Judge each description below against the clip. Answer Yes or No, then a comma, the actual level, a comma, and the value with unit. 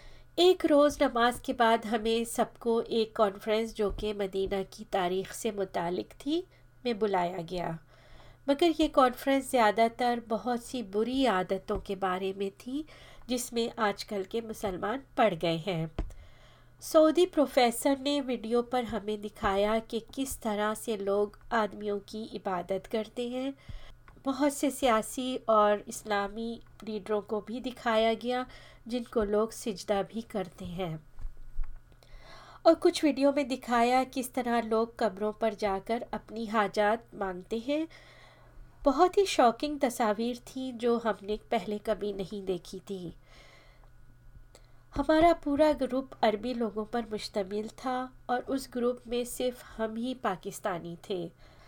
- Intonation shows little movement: No, average, 3.7 semitones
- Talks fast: No, average, 135 wpm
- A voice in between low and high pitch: No, high, 225 Hz